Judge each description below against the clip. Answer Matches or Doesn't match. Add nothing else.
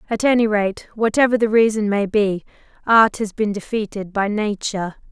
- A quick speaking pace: Doesn't match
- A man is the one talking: Doesn't match